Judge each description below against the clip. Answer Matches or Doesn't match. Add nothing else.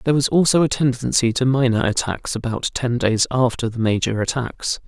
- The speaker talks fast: Doesn't match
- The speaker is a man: Matches